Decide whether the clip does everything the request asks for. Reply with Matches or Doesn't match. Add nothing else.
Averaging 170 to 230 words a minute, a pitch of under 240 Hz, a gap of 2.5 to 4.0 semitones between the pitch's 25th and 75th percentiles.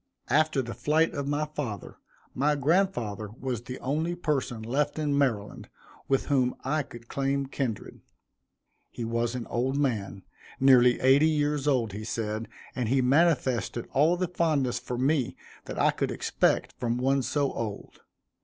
Doesn't match